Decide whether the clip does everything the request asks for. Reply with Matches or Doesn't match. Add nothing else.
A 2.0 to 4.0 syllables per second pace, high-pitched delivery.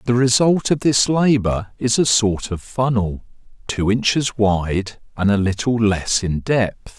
Doesn't match